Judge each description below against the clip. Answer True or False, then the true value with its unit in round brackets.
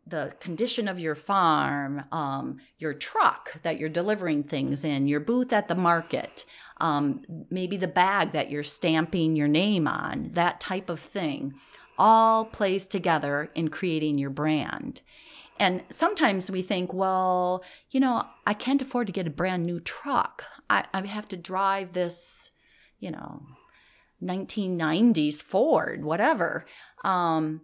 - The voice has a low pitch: False (180 Hz)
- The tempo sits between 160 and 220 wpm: False (145 wpm)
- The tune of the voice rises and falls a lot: False (4.0 semitones)